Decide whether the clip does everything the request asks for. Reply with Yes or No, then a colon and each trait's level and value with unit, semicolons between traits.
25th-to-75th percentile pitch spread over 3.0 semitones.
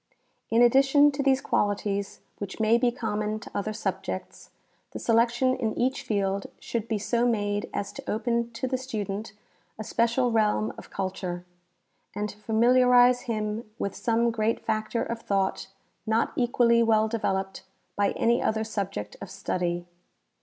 No: average, 2.7 semitones